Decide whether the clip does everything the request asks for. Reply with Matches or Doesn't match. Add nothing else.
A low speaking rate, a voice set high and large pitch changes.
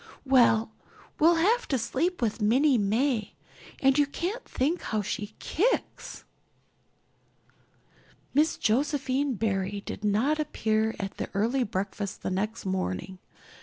Matches